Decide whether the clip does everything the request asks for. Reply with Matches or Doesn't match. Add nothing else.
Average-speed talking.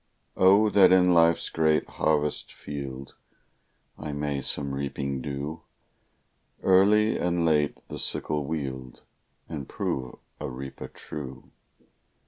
Doesn't match